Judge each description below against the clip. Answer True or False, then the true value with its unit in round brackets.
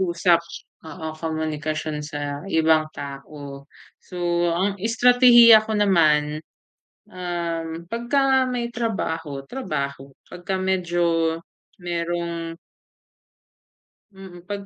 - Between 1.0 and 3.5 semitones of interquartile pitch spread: False (4.2 semitones)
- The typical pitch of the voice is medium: True (170 Hz)